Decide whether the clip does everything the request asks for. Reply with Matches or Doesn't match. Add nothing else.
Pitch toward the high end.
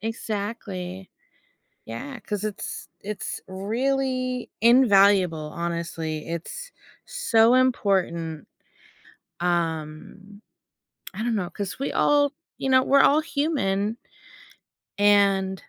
Matches